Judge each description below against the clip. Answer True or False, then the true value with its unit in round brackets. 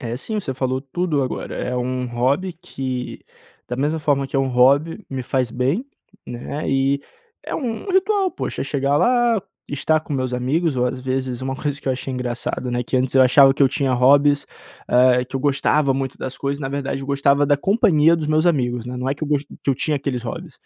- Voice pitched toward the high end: False (135 Hz)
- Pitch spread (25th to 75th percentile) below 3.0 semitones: True (2.6 semitones)